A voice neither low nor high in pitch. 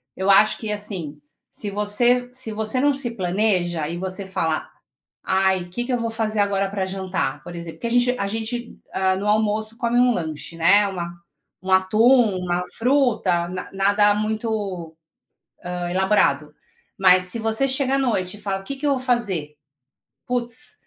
No: high, 205 Hz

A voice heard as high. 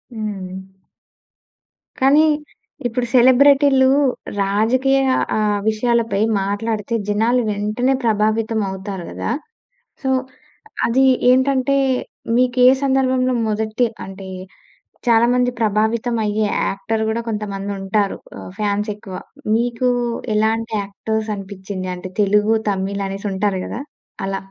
Yes: high, 220 Hz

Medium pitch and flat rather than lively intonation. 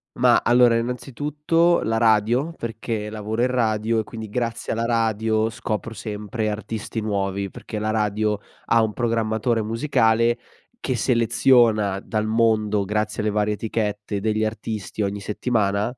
No: low, 110 Hz; narrow, 1.6 semitones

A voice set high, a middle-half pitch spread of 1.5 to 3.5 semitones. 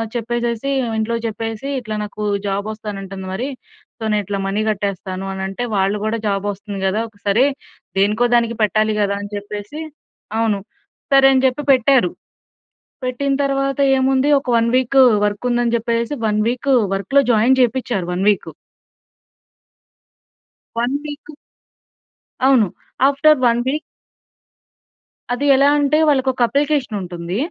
No: high, 230 Hz; average, 4.4 semitones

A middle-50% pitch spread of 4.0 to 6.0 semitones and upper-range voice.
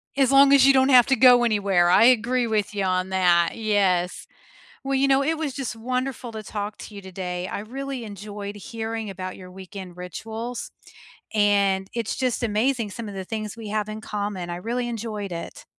Yes: average, 4.3 semitones; high, 215 Hz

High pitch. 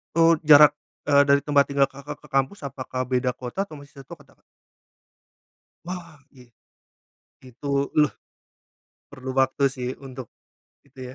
No: medium, 140 Hz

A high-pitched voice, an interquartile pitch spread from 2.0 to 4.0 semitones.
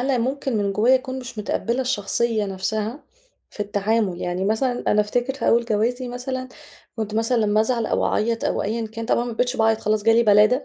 Yes: high, 225 Hz; average, 2.7 semitones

